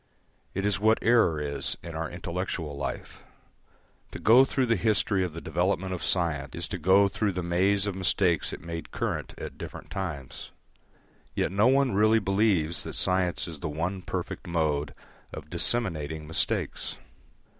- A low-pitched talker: Yes, very low, 90 Hz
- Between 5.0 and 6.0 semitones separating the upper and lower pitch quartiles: No, average, 3.9 semitones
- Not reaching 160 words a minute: No, average, 165 wpm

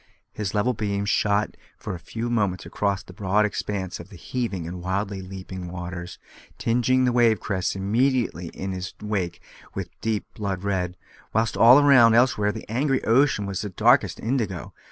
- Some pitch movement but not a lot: Yes, average, 3.7 semitones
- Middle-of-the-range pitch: No, low, 100 Hz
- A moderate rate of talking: Yes, average, 165 wpm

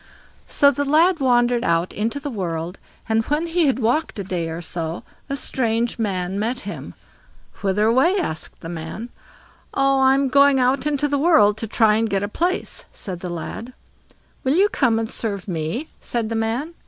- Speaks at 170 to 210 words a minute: Yes, average, 185 wpm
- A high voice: Yes, high, 230 Hz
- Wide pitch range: Yes, wide, 5.8 semitones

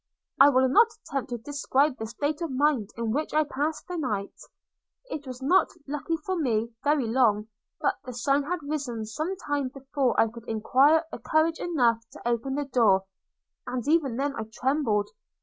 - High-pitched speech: Yes, very high, 270 Hz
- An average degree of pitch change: Yes, average, 4.2 semitones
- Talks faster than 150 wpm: Yes, average, 180 wpm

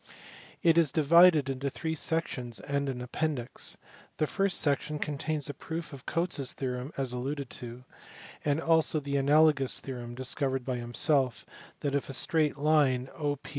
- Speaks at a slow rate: No, average, 160 wpm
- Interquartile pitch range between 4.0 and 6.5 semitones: No, average, 3.1 semitones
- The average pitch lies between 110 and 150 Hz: Yes, medium, 140 Hz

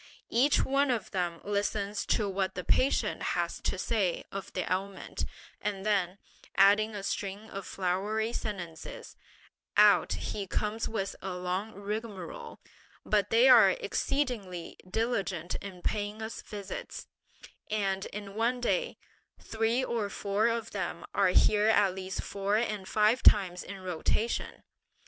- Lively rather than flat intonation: No, average, 2.7 semitones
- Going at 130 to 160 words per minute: Yes, average, 140 wpm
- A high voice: Yes, high, 205 Hz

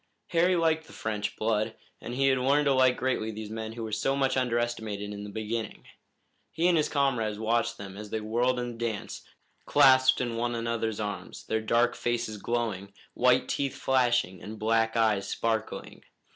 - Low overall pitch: Yes, low, 115 Hz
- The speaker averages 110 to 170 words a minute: No, average, 185 wpm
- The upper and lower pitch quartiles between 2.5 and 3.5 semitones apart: Yes, average, 2.8 semitones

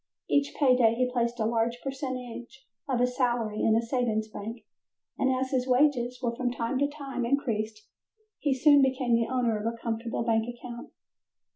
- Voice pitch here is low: No, high, 245 Hz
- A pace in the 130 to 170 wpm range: No, average, 180 wpm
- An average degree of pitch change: No, narrow, 2.1 semitones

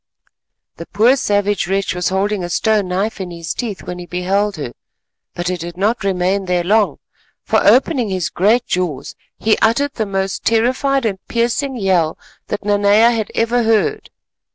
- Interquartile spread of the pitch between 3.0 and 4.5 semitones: Yes, average, 3.9 semitones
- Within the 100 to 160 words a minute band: No, average, 170 wpm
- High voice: Yes, high, 205 Hz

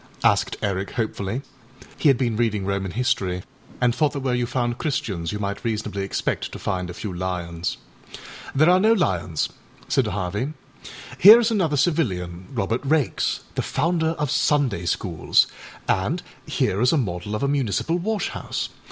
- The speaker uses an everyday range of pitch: No, wide, 7.6 semitones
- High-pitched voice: No, low, 115 Hz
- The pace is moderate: Yes, average, 170 wpm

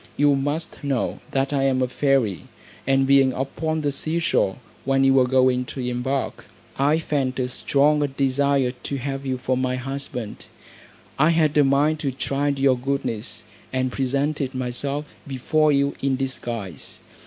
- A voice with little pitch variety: Yes, narrow, 1.7 semitones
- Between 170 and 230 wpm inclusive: No, average, 160 wpm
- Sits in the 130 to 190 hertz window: Yes, low, 135 Hz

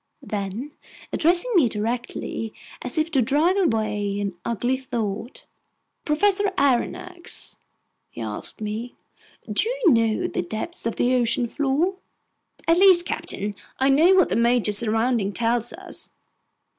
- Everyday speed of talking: No, slow, 130 wpm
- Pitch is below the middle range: No, high, 245 Hz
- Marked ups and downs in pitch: Yes, wide, 6.9 semitones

